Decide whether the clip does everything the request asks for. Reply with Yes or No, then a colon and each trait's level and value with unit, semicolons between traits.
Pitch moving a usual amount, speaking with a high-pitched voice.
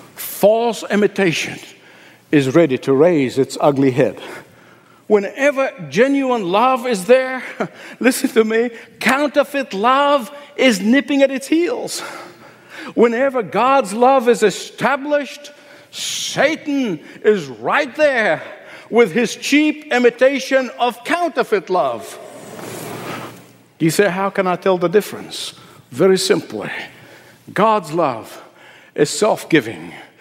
No: wide, 5.8 semitones; high, 240 Hz